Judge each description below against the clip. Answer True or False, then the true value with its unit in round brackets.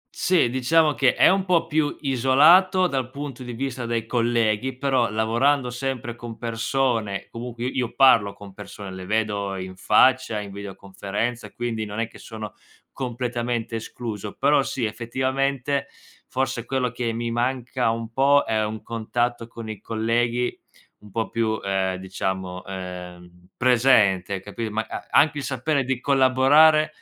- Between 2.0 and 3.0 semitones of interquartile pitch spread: False (3.6 semitones)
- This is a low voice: True (120 Hz)